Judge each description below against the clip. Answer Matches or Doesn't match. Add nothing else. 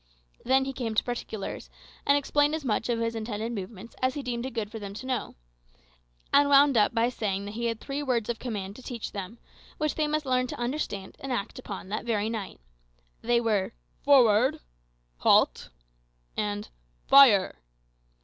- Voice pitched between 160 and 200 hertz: Doesn't match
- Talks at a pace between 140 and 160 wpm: Doesn't match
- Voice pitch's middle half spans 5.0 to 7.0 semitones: Doesn't match